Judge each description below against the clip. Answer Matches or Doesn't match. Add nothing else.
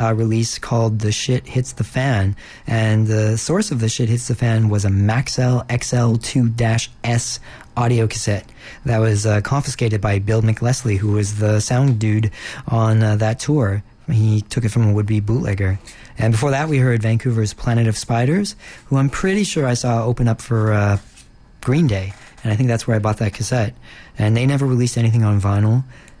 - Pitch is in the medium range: Doesn't match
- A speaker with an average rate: Matches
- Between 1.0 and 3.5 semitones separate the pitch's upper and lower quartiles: Matches